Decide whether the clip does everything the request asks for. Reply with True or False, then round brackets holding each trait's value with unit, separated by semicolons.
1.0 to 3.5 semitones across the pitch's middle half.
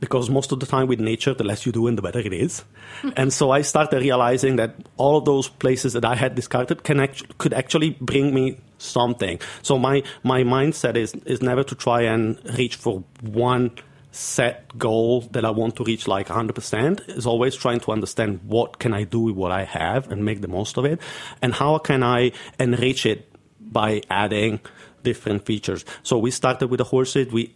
True (2.9 semitones)